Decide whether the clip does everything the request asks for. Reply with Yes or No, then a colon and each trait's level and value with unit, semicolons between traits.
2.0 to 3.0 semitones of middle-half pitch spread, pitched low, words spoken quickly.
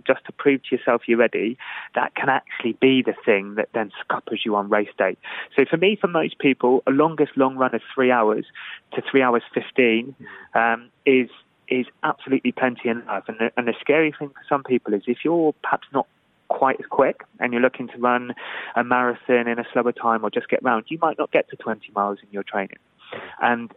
Yes: narrow, 2.6 semitones; low, 125 Hz; fast, 215 wpm